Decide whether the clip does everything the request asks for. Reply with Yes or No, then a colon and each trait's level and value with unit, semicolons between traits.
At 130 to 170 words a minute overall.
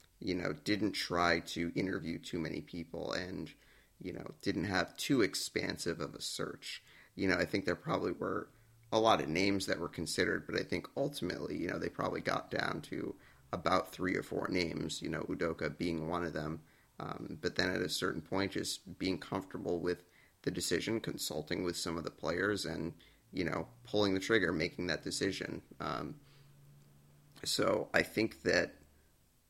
No: average, 180 wpm